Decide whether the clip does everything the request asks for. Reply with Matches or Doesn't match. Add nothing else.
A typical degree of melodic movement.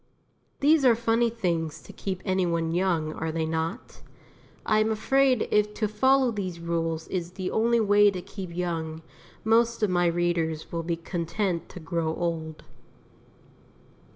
Matches